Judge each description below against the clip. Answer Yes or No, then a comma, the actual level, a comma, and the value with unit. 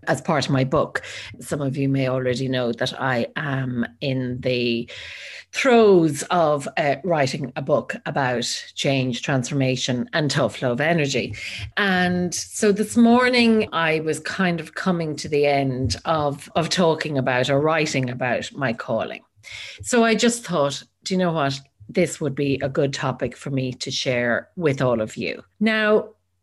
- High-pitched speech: No, medium, 140 Hz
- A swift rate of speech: No, average, 170 wpm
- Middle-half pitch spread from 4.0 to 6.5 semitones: Yes, average, 4.7 semitones